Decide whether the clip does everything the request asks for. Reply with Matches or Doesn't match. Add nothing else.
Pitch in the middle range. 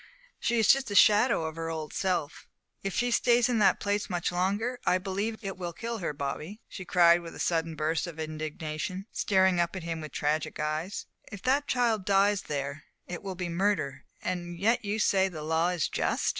Matches